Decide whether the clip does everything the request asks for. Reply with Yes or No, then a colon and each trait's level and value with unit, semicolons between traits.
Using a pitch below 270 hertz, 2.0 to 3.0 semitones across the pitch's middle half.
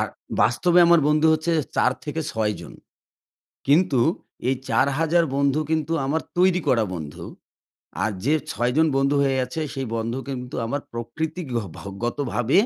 No: medium, 140 Hz; average, 4.6 semitones